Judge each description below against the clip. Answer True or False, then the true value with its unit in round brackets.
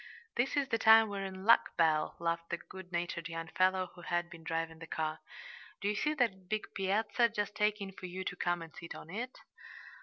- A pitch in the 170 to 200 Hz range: True (185 Hz)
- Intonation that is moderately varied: True (3.9 semitones)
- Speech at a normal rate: False (215 wpm)